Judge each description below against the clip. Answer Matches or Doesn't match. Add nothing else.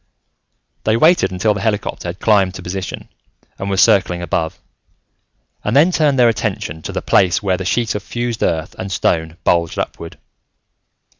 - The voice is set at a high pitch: Doesn't match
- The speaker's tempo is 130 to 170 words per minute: Matches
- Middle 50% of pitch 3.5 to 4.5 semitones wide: Matches